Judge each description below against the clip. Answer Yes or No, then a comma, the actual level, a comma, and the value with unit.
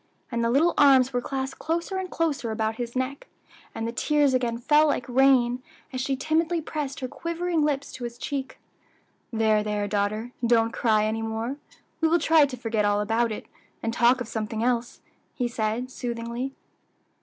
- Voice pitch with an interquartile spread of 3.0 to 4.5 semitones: Yes, average, 3.7 semitones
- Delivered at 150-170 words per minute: No, average, 180 wpm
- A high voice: Yes, high, 245 Hz